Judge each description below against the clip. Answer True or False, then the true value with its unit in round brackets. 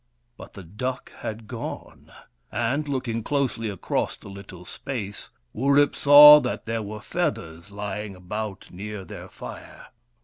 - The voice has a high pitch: False (110 Hz)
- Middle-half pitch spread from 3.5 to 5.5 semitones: True (4.6 semitones)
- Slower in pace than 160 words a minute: True (135 wpm)